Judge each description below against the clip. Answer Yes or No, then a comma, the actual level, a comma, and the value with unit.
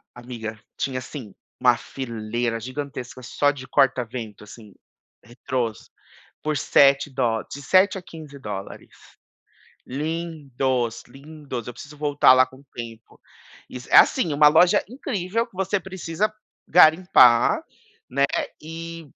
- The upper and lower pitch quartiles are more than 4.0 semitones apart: Yes, average, 5.0 semitones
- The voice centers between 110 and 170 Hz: Yes, low, 135 Hz